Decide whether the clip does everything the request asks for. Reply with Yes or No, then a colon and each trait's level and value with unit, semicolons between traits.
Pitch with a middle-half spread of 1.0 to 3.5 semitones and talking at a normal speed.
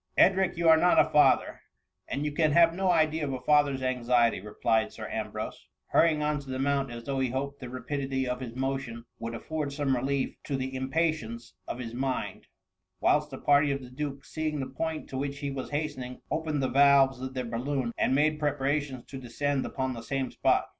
No: narrow, 2.5 semitones; fast, 215 wpm